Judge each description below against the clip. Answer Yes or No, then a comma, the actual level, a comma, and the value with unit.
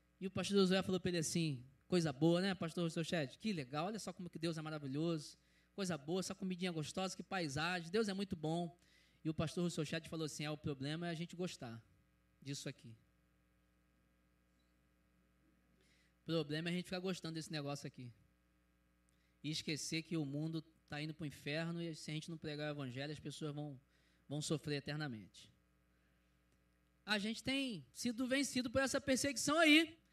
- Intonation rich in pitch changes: Yes, wide, 7.5 semitones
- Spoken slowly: No, fast, 185 wpm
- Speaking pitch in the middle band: Yes, medium, 155 Hz